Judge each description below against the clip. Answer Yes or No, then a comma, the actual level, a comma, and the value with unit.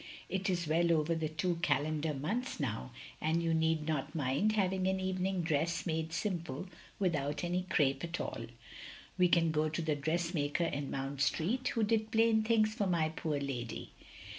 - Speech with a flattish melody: No, average, 3.7 semitones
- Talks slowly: No, average, 175 wpm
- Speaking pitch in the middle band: Yes, medium, 165 Hz